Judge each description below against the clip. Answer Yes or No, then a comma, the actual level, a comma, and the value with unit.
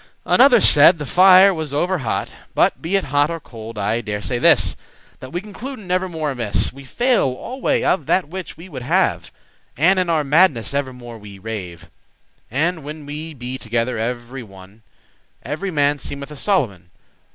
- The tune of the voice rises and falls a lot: Yes, wide, 7.0 semitones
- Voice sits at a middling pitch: Yes, medium, 145 Hz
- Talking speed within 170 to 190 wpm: Yes, average, 175 wpm